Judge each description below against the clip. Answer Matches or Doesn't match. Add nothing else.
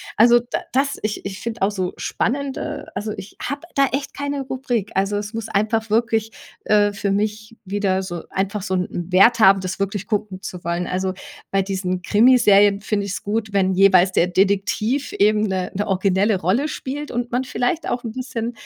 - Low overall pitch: Doesn't match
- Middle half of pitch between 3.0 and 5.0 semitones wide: Matches